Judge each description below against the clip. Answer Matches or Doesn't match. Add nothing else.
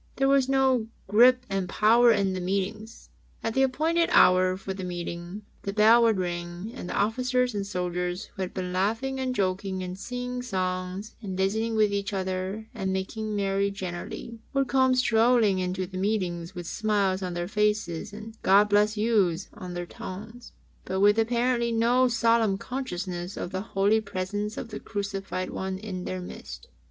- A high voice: Matches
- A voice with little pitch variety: Doesn't match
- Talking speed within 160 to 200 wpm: Matches